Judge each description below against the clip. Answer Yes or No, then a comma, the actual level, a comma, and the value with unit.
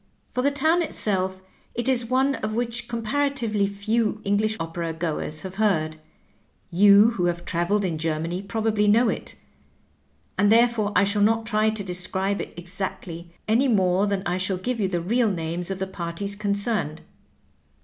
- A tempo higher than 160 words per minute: Yes, average, 170 wpm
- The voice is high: Yes, high, 200 Hz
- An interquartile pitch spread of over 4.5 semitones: No, average, 3.9 semitones